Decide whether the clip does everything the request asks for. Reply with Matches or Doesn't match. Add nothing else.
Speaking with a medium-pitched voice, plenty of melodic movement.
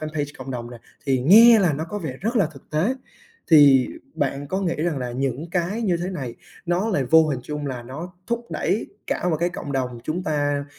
Doesn't match